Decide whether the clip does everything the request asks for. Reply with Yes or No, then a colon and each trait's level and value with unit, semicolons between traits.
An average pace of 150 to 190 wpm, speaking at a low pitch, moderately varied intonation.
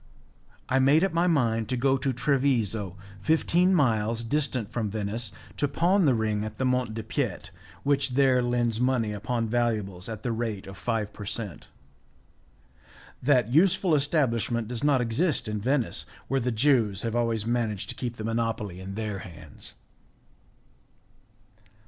Yes: average, 155 wpm; low, 115 Hz; average, 3.8 semitones